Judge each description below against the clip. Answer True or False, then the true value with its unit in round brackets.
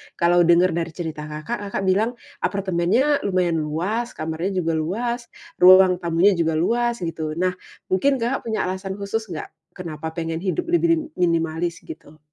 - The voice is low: False (180 Hz)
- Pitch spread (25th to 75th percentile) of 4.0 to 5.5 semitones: True (4.6 semitones)